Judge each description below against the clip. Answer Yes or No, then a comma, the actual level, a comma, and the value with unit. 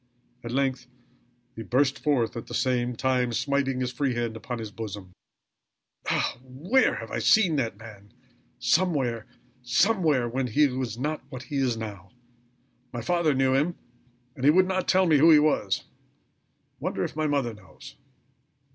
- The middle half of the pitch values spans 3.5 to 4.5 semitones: Yes, average, 4.1 semitones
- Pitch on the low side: Yes, low, 130 Hz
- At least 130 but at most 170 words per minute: Yes, average, 165 wpm